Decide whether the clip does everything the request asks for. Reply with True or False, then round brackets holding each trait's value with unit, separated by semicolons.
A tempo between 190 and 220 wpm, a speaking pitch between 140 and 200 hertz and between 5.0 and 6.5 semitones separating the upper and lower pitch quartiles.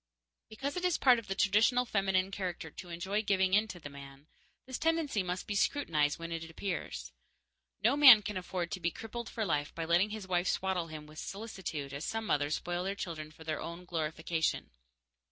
False (200 wpm; 185 Hz; 4.6 semitones)